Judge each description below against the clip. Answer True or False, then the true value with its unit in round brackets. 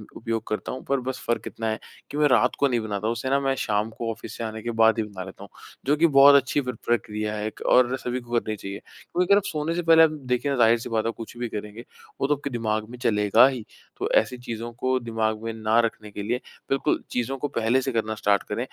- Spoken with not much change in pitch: False (3.2 semitones)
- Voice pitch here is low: True (120 Hz)